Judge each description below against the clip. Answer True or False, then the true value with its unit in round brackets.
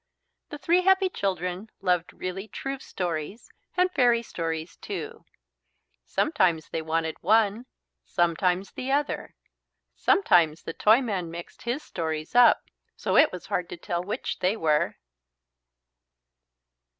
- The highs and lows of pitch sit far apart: True (6.2 semitones)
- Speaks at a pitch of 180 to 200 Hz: True (185 Hz)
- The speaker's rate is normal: False (125 wpm)